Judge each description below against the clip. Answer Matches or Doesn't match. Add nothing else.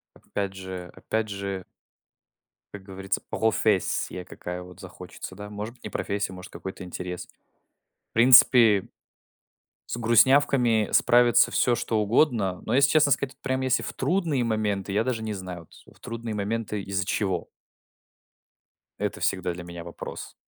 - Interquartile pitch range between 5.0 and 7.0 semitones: Doesn't match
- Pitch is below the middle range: Matches